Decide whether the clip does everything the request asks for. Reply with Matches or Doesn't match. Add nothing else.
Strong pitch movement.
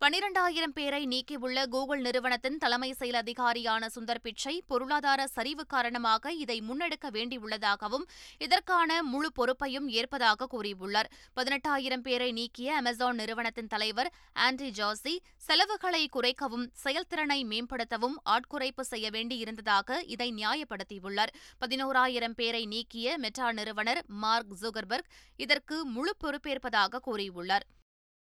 Doesn't match